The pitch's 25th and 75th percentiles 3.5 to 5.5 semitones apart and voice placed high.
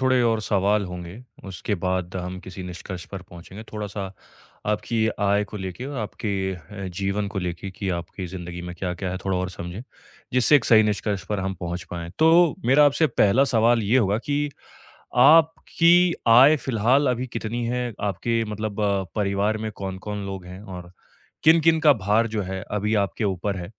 No: average, 3.9 semitones; low, 105 Hz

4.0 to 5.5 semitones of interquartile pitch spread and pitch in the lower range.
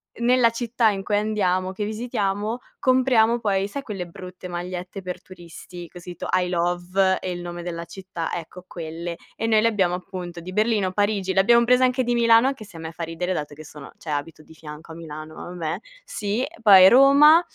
No: average, 4.3 semitones; medium, 185 Hz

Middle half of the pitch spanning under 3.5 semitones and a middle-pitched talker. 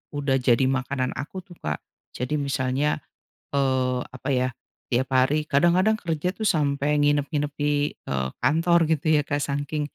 Yes: narrow, 2.6 semitones; medium, 145 Hz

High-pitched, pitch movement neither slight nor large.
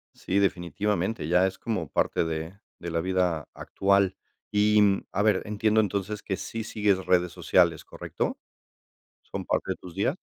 No: very low, 95 Hz; average, 3.0 semitones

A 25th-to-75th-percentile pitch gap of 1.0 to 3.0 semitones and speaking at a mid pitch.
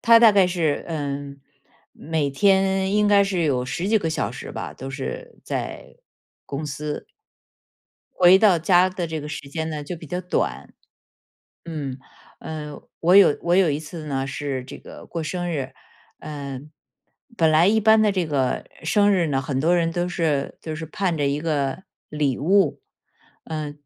No: average, 4.2 semitones; medium, 160 Hz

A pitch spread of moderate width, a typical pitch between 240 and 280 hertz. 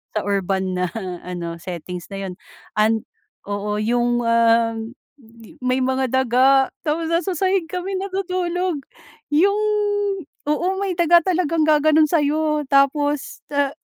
No: wide, 6.9 semitones; very high, 275 Hz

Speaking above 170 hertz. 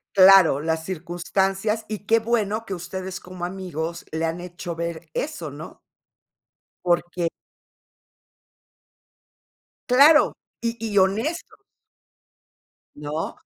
Yes: medium, 185 Hz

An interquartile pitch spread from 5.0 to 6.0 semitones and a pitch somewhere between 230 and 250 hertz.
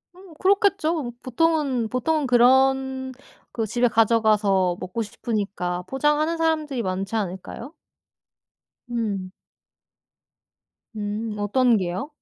Yes: wide, 5.4 semitones; high, 240 Hz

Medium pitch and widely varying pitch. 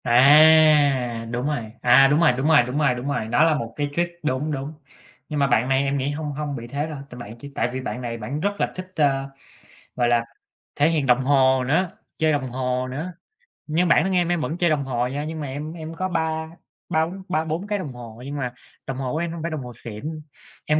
No: medium, 145 Hz; average, 3.8 semitones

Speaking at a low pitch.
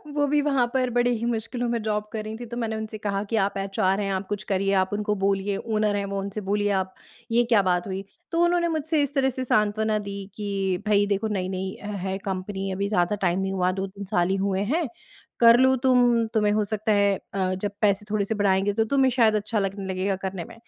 No: high, 205 Hz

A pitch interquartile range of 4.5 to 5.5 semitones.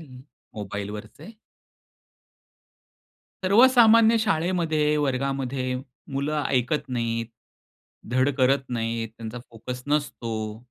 Yes: average, 5.1 semitones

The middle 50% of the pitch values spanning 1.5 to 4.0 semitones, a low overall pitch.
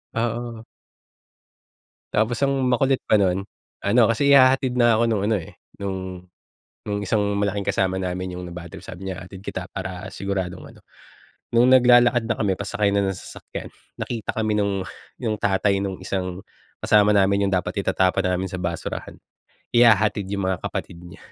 Yes: average, 3.3 semitones; low, 100 Hz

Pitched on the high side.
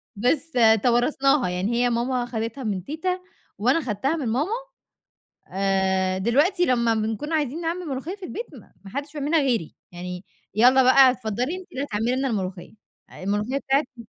Yes: very high, 250 Hz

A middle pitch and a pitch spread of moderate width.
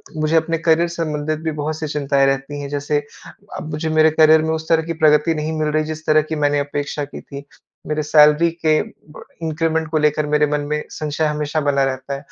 No: medium, 155 Hz; narrow, 1.4 semitones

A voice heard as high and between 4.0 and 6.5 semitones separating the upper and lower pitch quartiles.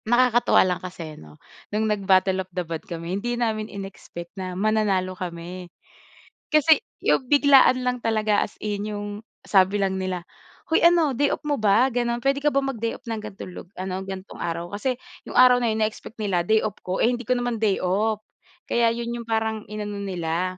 Yes: high, 210 Hz; average, 4.3 semitones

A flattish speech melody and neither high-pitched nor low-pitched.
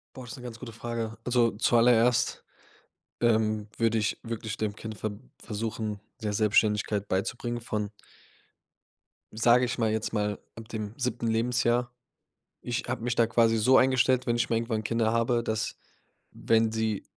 No: narrow, 1.6 semitones; low, 115 Hz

